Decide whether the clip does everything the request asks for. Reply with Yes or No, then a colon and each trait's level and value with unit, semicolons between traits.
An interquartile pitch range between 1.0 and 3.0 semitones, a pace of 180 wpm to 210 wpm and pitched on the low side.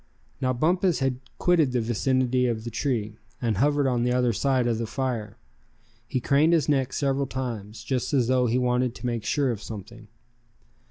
Yes: narrow, 2.5 semitones; average, 185 wpm; low, 125 Hz